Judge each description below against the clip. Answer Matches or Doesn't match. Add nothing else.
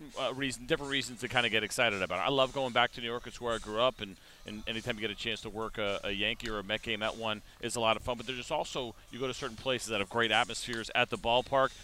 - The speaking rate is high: Matches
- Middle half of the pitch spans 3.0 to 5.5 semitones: Doesn't match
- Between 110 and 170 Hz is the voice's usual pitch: Matches